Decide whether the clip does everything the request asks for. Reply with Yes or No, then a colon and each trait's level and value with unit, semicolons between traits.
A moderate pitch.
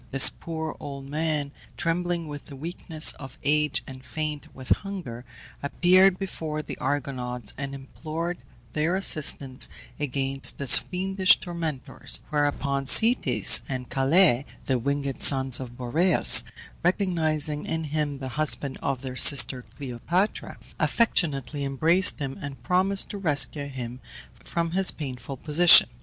Yes: medium, 145 Hz